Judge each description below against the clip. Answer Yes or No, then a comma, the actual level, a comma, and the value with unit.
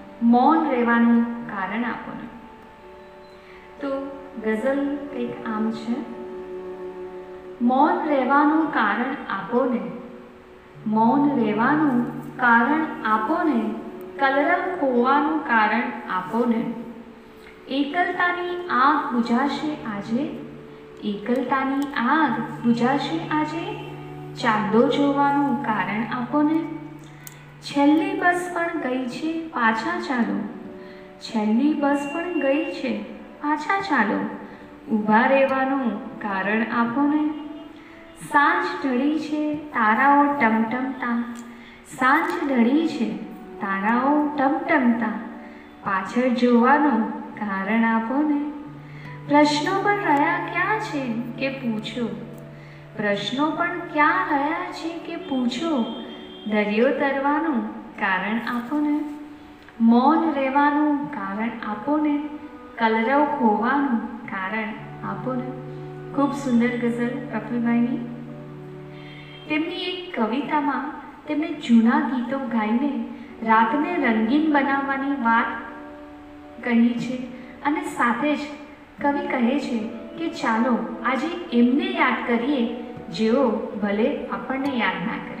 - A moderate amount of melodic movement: Yes, average, 4.5 semitones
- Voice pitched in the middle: No, very high, 255 Hz